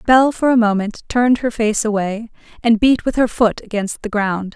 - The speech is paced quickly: Yes, fast, 210 wpm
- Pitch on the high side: Yes, high, 225 Hz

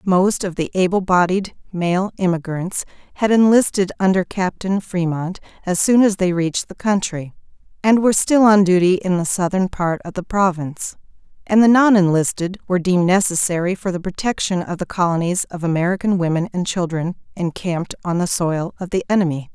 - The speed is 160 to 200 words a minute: Yes, average, 170 wpm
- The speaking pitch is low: No, medium, 185 Hz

